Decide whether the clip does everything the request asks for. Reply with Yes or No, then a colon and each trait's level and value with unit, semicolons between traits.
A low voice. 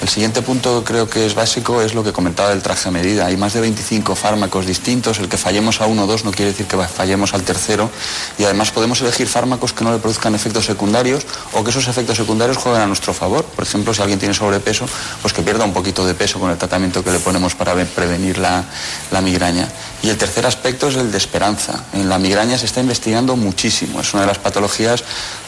Yes: low, 105 Hz